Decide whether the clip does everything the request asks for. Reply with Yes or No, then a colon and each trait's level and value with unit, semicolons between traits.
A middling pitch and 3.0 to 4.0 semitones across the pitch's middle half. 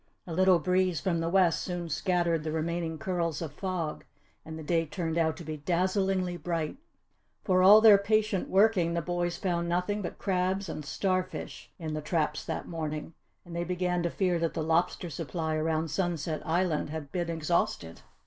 No: medium, 170 Hz; narrow, 2.4 semitones